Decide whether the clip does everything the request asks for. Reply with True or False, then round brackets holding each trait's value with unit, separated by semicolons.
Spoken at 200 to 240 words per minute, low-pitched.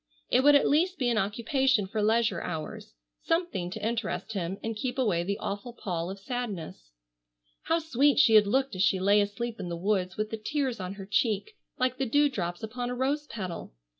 False (205 wpm; 220 Hz)